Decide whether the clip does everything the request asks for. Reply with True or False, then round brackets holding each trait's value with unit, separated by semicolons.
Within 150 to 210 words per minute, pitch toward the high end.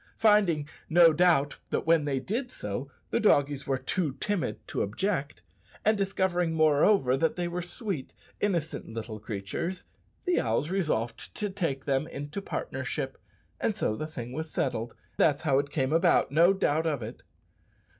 False (160 wpm; 155 Hz)